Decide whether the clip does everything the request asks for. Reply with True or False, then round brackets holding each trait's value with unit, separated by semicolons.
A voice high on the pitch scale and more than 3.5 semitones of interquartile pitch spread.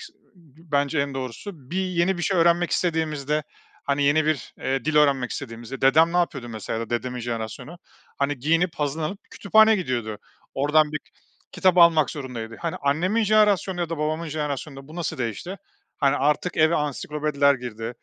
False (150 Hz; 4.2 semitones)